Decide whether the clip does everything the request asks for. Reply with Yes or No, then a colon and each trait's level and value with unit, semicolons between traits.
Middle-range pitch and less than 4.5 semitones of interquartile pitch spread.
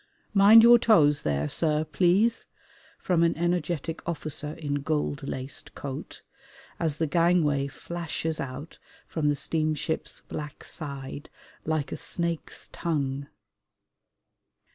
Yes: medium, 155 Hz; average, 2.9 semitones